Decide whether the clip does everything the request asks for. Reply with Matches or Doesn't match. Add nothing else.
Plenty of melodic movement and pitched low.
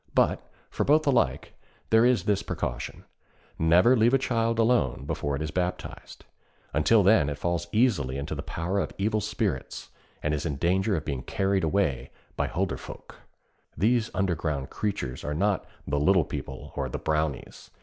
Matches